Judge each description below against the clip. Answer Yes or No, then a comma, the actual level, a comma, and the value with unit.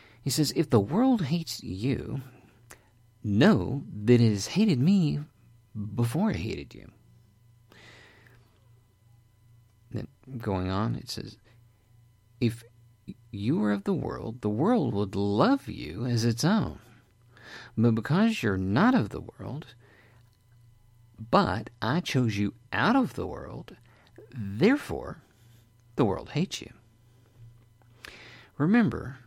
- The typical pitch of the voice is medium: No, low, 115 Hz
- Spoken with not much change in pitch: Yes, narrow, 2.2 semitones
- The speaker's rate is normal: No, slow, 115 wpm